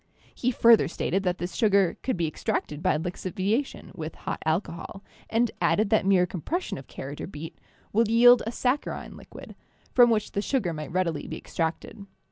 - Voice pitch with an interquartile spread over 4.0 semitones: Yes, wide, 5.4 semitones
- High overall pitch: Yes, high, 195 Hz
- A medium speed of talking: Yes, average, 185 wpm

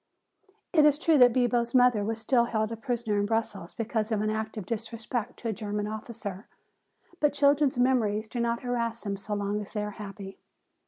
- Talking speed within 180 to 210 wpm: Yes, average, 200 wpm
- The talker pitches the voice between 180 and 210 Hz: No, high, 225 Hz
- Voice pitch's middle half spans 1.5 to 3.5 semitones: Yes, narrow, 2.6 semitones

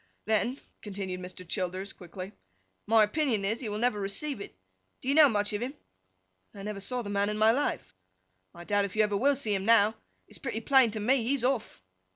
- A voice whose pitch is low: No, high, 210 Hz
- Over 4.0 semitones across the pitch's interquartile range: No, average, 3.7 semitones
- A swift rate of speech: Yes, fast, 210 wpm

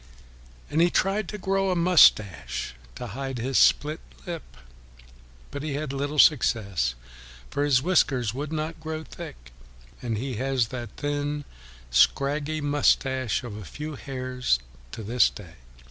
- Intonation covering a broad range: No, average, 4.1 semitones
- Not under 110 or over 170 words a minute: Yes, average, 145 wpm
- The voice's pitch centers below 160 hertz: Yes, medium, 140 Hz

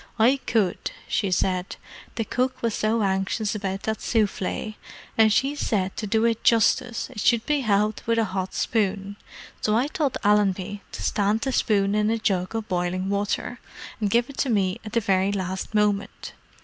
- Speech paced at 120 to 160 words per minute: No, average, 185 wpm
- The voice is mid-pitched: No, high, 210 Hz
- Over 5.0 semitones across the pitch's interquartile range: No, average, 2.7 semitones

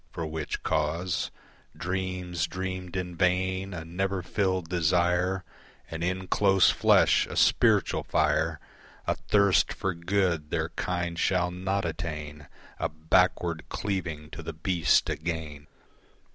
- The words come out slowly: Yes, slow, 125 wpm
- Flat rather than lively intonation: Yes, narrow, 2.2 semitones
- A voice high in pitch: No, very low, 90 Hz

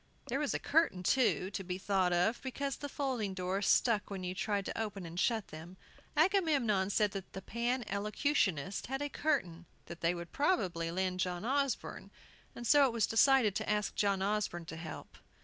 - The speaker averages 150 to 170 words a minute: No, average, 185 wpm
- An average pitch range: No, wide, 6.1 semitones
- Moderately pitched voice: No, high, 205 Hz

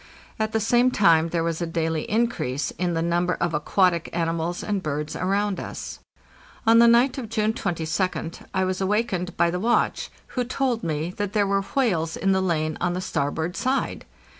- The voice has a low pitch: No, medium, 185 Hz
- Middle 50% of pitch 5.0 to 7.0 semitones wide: No, average, 4.6 semitones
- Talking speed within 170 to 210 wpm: Yes, average, 190 wpm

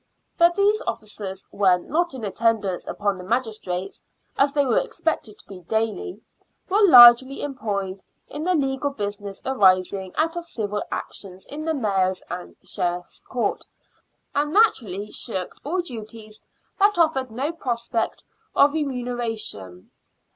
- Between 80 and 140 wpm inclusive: Yes, slow, 135 wpm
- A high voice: Yes, high, 230 Hz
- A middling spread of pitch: No, wide, 6.6 semitones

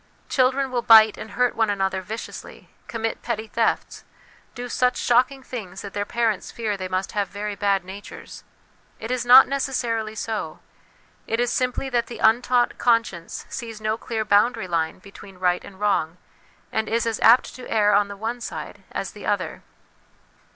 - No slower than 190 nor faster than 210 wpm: No, average, 170 wpm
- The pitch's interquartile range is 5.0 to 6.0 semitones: No, average, 3.1 semitones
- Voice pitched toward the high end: Yes, high, 220 Hz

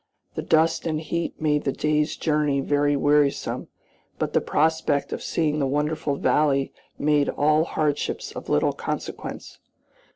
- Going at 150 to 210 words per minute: No, average, 140 wpm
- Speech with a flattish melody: Yes, narrow, 1.4 semitones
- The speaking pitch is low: No, medium, 150 Hz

